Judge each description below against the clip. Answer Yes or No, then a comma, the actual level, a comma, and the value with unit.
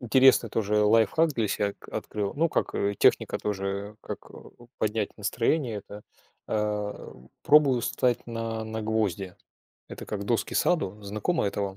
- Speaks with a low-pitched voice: Yes, low, 105 Hz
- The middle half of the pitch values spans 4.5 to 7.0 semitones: No, narrow, 2.6 semitones